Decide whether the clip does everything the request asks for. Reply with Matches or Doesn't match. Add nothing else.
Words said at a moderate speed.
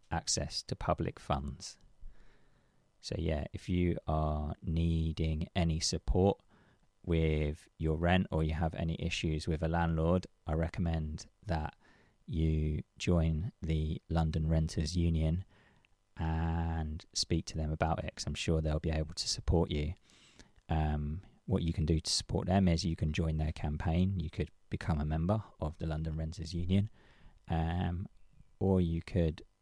Matches